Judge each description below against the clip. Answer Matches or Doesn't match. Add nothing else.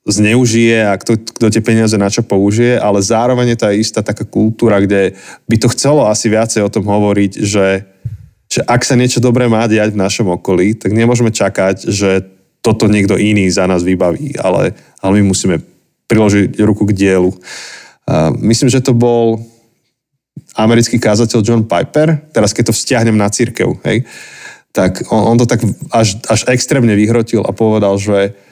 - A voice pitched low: Matches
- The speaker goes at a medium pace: Doesn't match